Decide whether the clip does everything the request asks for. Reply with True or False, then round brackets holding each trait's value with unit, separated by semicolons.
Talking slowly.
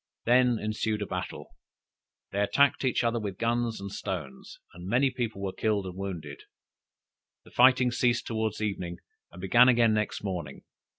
False (160 wpm)